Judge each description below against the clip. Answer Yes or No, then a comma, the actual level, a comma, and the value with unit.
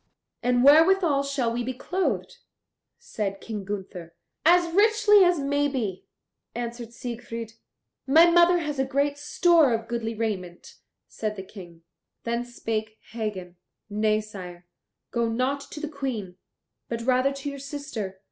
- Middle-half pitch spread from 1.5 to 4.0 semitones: No, average, 5.1 semitones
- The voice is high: Yes, high, 240 Hz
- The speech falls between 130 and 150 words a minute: Yes, average, 140 wpm